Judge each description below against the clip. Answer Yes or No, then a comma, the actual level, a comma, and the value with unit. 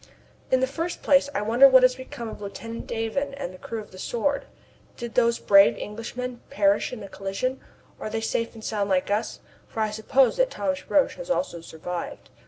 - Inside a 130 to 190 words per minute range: No, average, 200 wpm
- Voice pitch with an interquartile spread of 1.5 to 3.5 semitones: No, average, 4.3 semitones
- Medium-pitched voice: No, high, 230 Hz